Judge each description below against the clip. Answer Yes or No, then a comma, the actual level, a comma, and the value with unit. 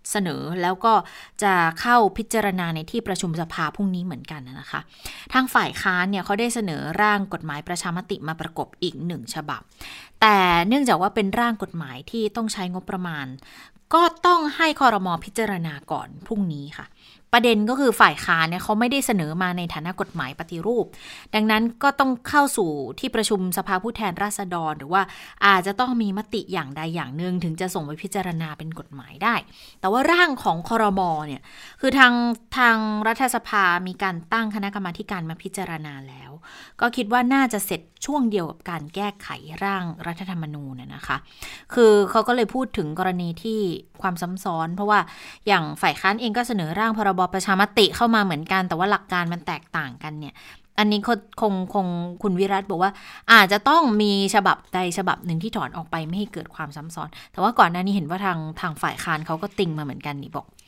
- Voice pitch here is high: Yes, high, 195 Hz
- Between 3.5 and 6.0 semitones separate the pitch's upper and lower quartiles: Yes, average, 4.7 semitones